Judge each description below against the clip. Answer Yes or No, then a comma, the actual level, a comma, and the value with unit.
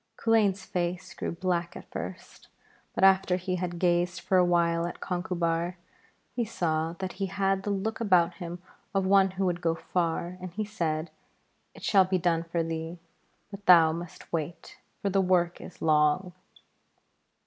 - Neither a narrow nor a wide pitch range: No, narrow, 2.1 semitones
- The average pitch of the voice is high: No, medium, 180 Hz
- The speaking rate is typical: Yes, average, 170 wpm